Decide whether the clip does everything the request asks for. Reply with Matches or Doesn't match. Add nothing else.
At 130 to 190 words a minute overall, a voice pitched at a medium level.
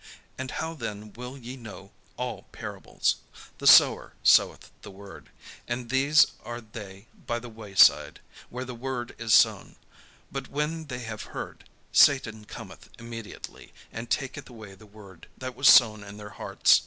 Doesn't match